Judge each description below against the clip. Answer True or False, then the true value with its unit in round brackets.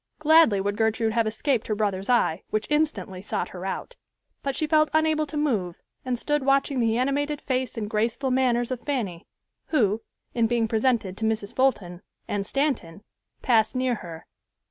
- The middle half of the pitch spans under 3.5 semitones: False (4.7 semitones)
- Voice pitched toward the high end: True (235 Hz)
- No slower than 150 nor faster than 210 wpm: True (170 wpm)